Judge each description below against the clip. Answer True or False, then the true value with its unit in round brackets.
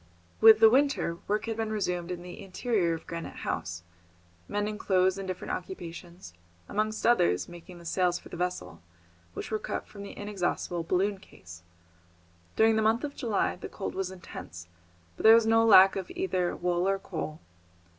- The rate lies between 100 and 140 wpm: False (175 wpm)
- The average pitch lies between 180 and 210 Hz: True (190 Hz)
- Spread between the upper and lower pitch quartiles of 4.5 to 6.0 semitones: False (3.7 semitones)